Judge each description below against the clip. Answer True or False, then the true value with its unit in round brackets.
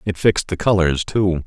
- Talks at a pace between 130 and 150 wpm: False (205 wpm)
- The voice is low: True (90 Hz)